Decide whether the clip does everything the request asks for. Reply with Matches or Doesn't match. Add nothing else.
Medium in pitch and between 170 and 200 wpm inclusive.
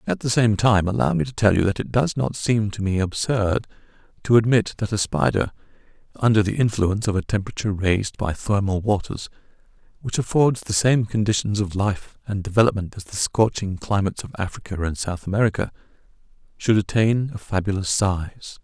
Doesn't match